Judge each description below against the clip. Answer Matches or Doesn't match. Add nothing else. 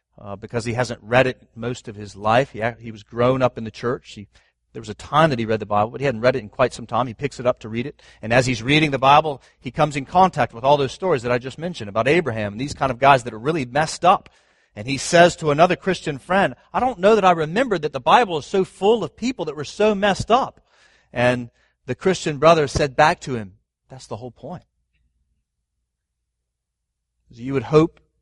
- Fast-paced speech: Matches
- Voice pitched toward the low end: Matches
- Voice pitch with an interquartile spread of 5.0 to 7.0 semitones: Matches